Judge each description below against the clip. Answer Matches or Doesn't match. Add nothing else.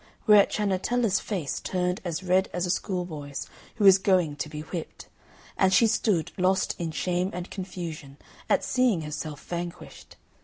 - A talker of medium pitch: Matches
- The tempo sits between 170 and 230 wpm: Doesn't match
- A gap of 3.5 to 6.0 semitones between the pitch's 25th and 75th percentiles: Doesn't match